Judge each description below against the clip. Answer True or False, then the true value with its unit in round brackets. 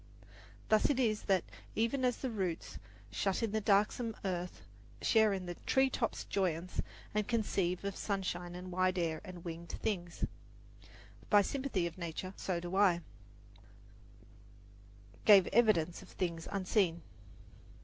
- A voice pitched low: False (190 Hz)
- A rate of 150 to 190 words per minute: False (140 wpm)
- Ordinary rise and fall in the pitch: True (3.5 semitones)